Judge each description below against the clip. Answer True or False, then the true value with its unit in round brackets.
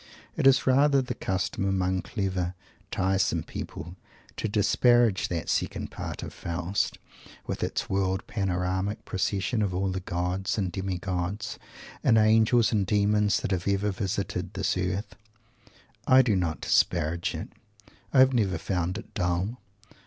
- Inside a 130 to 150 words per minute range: True (145 wpm)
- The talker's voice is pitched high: False (95 Hz)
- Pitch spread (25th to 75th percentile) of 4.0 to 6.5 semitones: False (2.9 semitones)